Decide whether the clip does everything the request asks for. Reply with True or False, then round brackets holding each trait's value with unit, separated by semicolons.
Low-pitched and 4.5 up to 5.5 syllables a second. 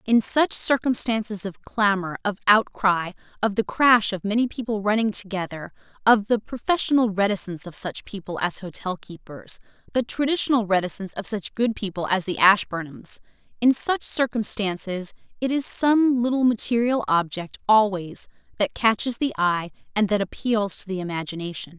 False (210 Hz; 5.0 syllables/s)